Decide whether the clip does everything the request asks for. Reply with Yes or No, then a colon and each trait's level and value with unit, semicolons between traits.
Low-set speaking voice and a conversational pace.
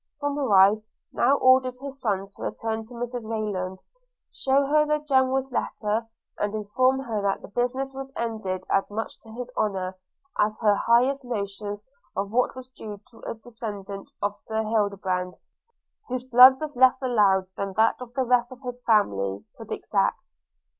No: high, 225 Hz; average, 165 wpm